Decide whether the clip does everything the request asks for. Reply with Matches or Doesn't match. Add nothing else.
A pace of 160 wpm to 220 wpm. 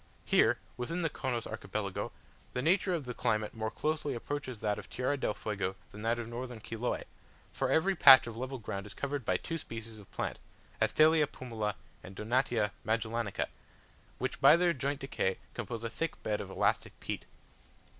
Matches